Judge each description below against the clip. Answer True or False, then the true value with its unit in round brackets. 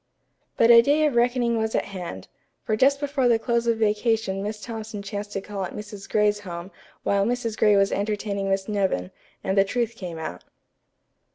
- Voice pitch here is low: False (210 Hz)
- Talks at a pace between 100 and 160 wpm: False (190 wpm)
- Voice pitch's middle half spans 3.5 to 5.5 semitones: False (2.9 semitones)